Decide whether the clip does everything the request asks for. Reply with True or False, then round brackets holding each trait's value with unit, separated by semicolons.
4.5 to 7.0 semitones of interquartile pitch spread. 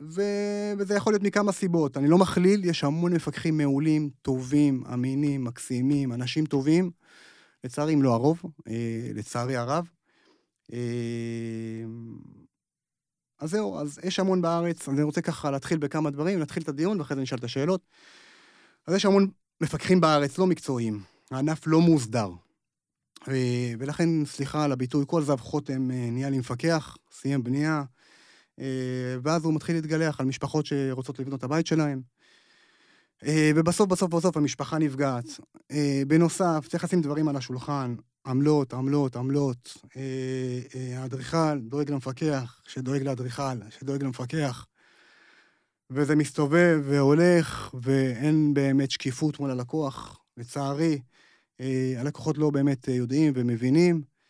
False (3.7 semitones)